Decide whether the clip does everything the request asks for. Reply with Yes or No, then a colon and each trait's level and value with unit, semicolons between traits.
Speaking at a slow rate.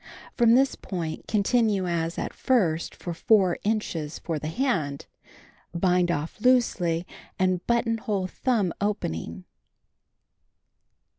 Yes: slow, 105 wpm